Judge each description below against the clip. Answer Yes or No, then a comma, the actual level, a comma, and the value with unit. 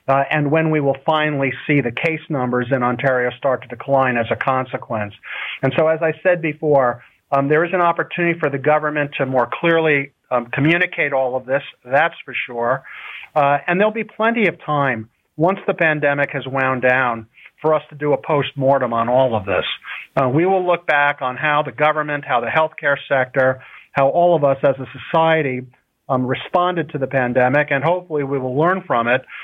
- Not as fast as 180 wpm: No, average, 200 wpm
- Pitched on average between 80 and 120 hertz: No, medium, 140 Hz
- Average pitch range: Yes, average, 3.3 semitones